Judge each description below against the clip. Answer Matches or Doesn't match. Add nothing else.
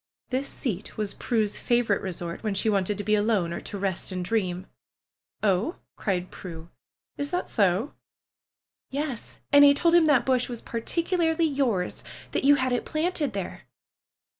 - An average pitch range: Doesn't match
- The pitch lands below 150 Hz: Doesn't match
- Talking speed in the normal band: Matches